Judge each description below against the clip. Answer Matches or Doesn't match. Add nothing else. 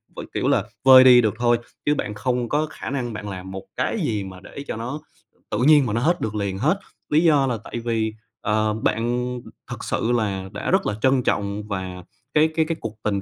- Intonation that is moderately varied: Matches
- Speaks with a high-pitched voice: Doesn't match